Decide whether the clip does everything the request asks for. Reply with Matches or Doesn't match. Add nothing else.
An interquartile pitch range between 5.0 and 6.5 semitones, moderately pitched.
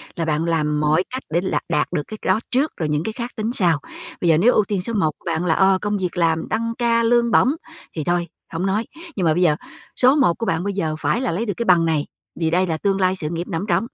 Matches